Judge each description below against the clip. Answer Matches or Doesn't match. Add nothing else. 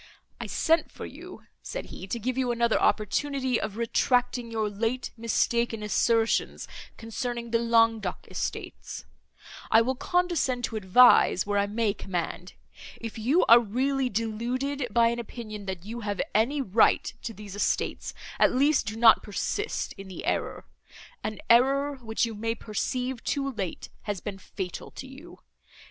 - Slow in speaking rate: Doesn't match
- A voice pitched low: Doesn't match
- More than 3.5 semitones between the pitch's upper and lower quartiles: Doesn't match